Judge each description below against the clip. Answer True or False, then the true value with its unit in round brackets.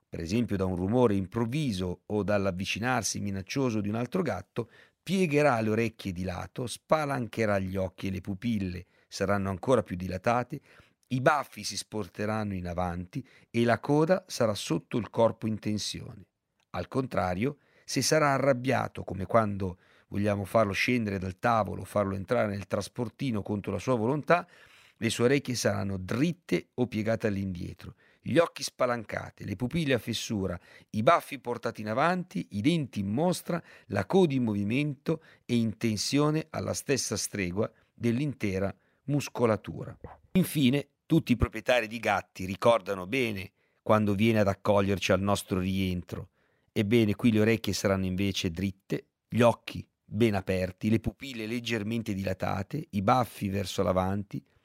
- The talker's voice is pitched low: True (110 Hz)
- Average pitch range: True (4.3 semitones)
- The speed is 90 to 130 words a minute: False (145 wpm)